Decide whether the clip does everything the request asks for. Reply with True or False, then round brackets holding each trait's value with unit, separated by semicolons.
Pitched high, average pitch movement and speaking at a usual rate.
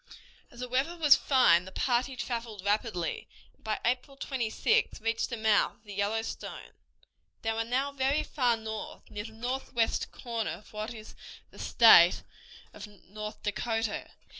True (225 Hz; 3.0 semitones; 155 wpm)